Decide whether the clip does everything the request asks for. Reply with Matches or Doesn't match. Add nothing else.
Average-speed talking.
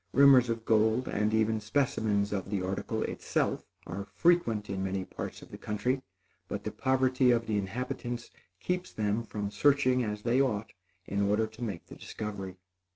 Matches